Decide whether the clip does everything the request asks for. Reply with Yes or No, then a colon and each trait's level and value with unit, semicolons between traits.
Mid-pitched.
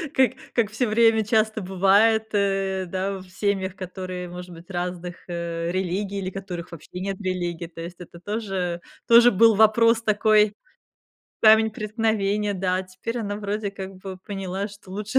No: high, 195 Hz